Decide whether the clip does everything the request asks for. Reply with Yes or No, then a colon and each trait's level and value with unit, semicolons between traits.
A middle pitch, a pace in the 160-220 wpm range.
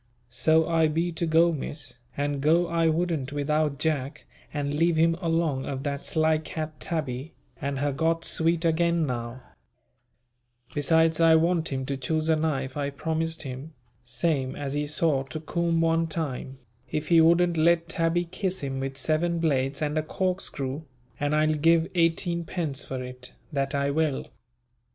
Yes: medium, 155 Hz; average, 165 wpm